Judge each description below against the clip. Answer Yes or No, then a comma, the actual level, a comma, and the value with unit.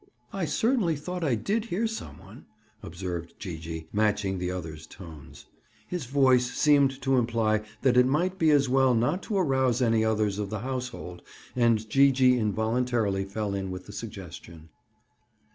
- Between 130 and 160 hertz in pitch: No, low, 120 Hz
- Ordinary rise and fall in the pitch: No, wide, 5.8 semitones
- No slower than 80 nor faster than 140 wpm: No, average, 165 wpm